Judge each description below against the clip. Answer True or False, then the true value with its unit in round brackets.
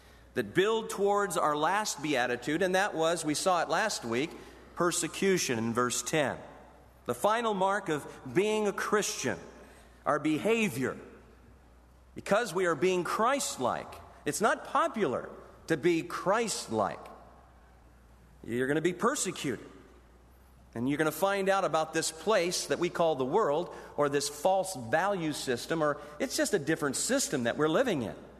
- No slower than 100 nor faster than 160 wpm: True (155 wpm)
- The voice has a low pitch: False (160 Hz)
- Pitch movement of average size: False (7.4 semitones)